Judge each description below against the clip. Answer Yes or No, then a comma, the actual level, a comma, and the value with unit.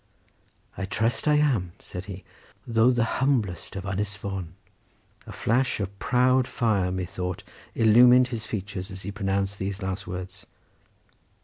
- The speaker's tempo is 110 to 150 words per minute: Yes, average, 140 wpm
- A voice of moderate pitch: No, low, 100 Hz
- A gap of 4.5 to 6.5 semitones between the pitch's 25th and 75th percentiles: No, average, 3.8 semitones